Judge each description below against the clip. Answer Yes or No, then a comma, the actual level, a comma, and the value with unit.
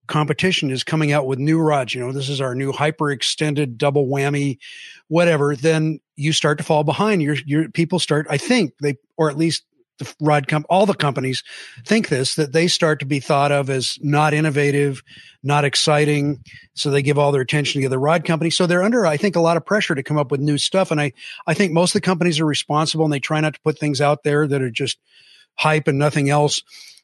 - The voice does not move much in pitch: Yes, narrow, 2.1 semitones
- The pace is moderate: No, fast, 235 wpm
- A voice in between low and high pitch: Yes, medium, 150 Hz